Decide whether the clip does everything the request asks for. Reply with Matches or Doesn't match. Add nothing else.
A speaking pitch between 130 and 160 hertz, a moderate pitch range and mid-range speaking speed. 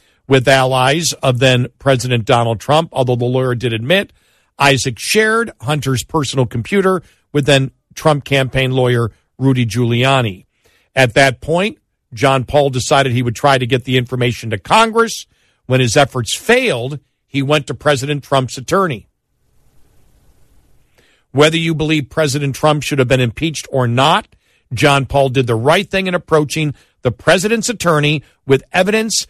Matches